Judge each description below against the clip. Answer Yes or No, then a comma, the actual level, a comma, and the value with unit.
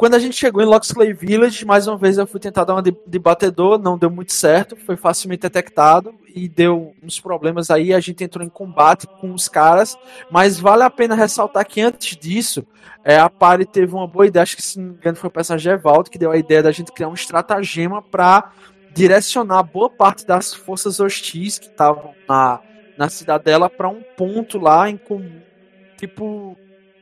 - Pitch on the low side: No, medium, 185 Hz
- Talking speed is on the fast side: Yes, fast, 200 wpm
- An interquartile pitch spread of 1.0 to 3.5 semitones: Yes, average, 3.0 semitones